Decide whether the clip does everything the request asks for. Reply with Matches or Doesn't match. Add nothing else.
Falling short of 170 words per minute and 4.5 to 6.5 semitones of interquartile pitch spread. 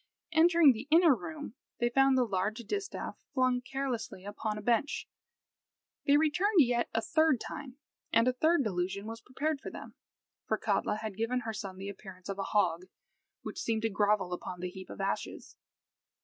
Doesn't match